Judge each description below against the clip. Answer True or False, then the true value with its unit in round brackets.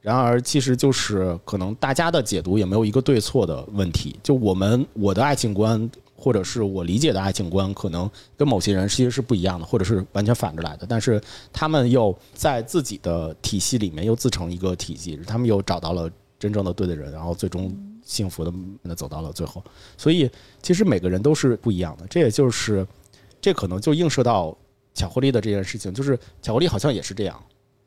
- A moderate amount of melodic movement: True (4.8 semitones)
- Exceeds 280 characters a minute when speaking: True (325 characters per minute)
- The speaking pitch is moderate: False (100 Hz)